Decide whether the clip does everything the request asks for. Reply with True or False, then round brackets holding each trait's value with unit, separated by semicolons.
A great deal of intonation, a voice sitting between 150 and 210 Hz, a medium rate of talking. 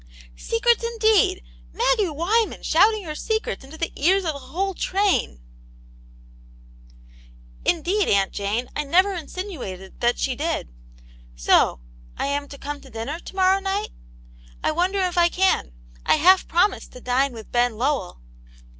False (6.9 semitones; 330 Hz; 155 wpm)